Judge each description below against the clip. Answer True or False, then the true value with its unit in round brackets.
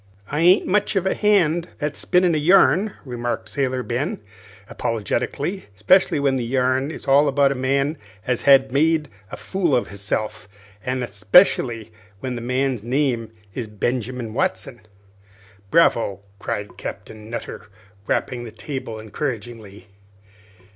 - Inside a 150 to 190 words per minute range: False (140 wpm)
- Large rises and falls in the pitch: False (4.6 semitones)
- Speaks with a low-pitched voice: True (130 Hz)